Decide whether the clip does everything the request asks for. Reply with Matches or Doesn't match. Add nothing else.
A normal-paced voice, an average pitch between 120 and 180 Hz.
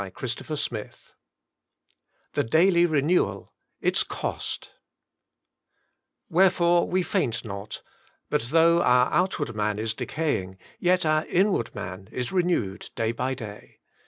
Doesn't match